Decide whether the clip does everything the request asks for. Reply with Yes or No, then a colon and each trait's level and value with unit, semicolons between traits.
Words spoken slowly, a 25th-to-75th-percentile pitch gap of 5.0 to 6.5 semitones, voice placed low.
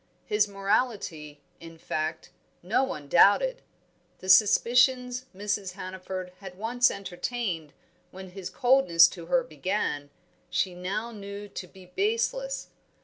No: slow, 120 wpm; average, 5.3 semitones; high, 195 Hz